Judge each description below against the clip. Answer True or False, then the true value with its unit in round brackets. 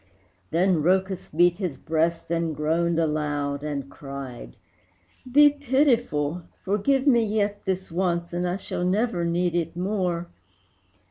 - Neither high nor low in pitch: True (175 Hz)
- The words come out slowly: True (130 wpm)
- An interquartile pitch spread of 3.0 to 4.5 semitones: True (3.8 semitones)